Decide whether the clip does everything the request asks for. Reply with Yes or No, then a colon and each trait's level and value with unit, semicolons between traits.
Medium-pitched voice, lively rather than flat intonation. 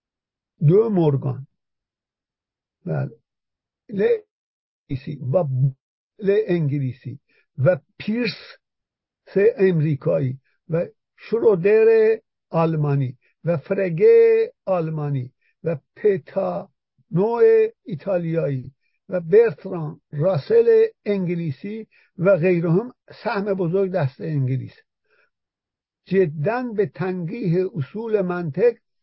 Yes: medium, 180 Hz; wide, 7.1 semitones